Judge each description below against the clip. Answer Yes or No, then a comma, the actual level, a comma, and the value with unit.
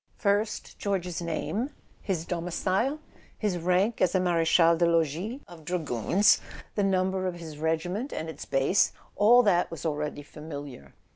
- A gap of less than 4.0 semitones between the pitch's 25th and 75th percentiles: Yes, average, 3.5 semitones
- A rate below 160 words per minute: Yes, average, 150 wpm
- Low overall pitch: No, medium, 175 Hz